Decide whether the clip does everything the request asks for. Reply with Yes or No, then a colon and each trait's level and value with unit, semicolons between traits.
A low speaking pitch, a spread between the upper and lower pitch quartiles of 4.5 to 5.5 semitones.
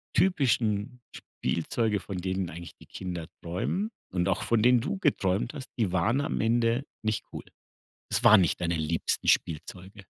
Yes: low, 105 Hz; average, 5.0 semitones